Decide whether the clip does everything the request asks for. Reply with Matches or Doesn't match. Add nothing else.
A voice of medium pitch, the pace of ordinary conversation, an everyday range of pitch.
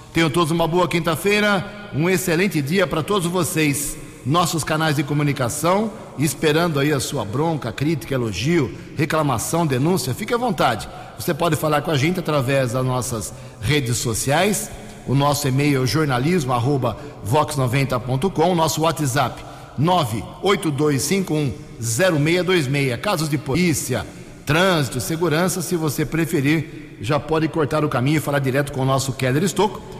Matches